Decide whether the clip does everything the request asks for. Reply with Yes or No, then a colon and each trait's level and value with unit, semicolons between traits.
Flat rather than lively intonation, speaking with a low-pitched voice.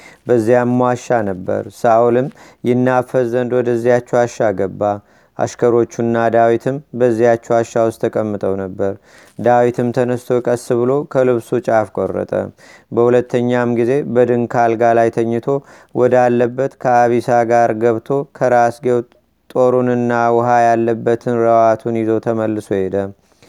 Yes: narrow, 1.3 semitones; low, 120 Hz